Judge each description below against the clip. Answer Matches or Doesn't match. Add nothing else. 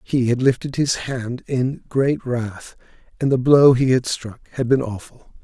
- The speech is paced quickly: Doesn't match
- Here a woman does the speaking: Doesn't match